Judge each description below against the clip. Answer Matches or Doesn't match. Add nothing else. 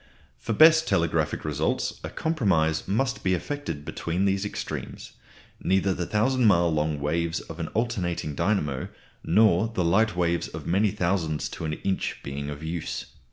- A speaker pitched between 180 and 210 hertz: Doesn't match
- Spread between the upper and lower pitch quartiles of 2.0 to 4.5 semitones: Doesn't match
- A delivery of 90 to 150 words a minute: Doesn't match